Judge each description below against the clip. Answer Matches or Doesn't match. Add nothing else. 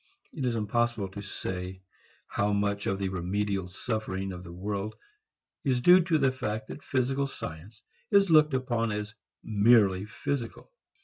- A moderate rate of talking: Matches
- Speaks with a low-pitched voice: Matches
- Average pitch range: Matches